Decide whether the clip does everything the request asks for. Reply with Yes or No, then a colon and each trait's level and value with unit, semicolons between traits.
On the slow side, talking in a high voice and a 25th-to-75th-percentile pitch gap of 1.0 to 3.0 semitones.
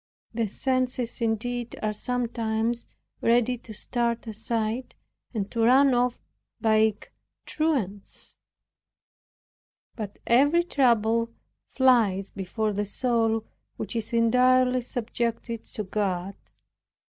Yes: slow, 100 wpm; high, 230 Hz; narrow, 2.4 semitones